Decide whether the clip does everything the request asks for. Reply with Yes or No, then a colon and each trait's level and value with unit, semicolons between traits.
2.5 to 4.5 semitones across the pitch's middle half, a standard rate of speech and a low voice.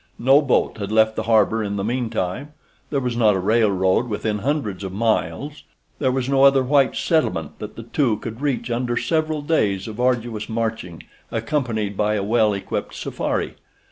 Yes: average, 3.9 semitones; average, 170 wpm; low, 115 Hz